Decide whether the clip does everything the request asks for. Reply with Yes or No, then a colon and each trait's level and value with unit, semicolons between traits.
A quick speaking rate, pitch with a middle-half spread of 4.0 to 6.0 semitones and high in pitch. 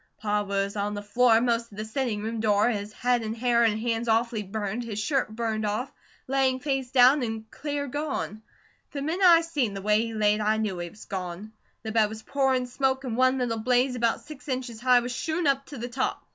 No: fast, 225 wpm; average, 3.4 semitones; high, 235 Hz